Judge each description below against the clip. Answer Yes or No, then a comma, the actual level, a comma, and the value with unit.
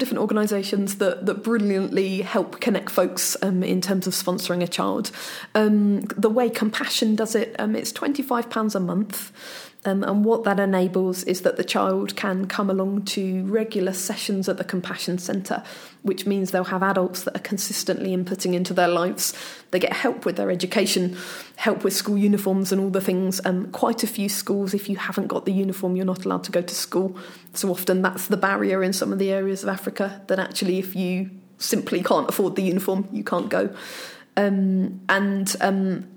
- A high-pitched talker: Yes, high, 195 Hz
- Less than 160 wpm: No, average, 195 wpm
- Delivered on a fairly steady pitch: Yes, narrow, 1.8 semitones